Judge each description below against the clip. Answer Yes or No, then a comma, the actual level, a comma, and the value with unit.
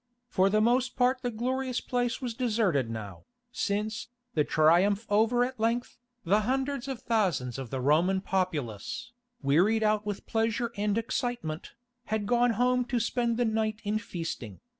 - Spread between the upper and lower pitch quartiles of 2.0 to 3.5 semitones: No, average, 4.8 semitones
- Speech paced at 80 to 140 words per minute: No, average, 160 wpm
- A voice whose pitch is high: Yes, high, 220 Hz